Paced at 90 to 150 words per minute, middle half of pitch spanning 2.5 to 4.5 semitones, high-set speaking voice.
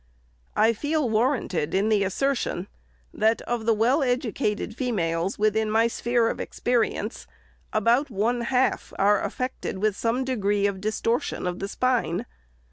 Yes: average, 140 wpm; average, 3.5 semitones; high, 225 Hz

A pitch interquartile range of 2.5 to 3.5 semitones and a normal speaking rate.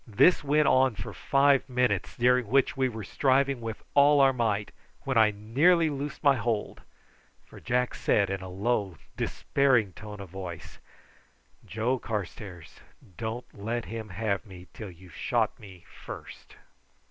No: average, 4.8 semitones; average, 150 wpm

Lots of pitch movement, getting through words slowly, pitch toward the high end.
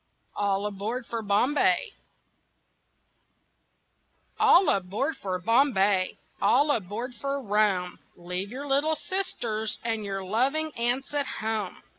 Yes: wide, 5.7 semitones; slow, 110 wpm; high, 225 Hz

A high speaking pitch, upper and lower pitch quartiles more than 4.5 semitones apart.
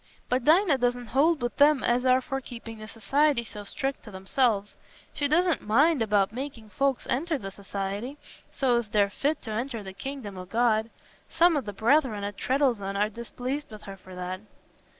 Yes: high, 240 Hz; average, 5.0 semitones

